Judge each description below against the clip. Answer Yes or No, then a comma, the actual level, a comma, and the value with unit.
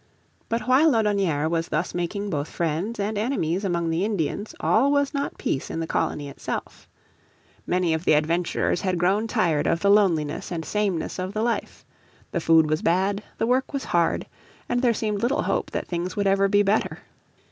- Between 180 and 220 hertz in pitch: Yes, high, 190 Hz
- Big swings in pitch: No, average, 4.5 semitones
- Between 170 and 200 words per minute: Yes, average, 190 wpm